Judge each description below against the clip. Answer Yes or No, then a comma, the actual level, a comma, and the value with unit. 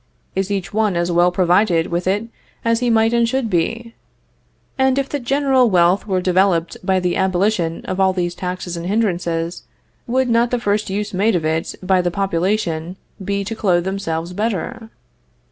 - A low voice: No, high, 190 Hz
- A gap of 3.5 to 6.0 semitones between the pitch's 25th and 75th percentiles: Yes, average, 4.1 semitones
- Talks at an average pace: Yes, average, 180 wpm